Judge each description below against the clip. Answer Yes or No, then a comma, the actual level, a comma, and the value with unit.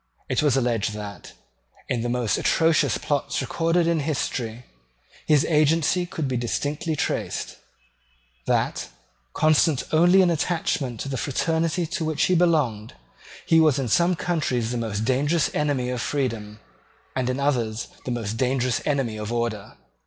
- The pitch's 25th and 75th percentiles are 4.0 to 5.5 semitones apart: Yes, average, 5.1 semitones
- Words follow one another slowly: No, average, 150 wpm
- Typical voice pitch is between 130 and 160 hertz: Yes, low, 135 Hz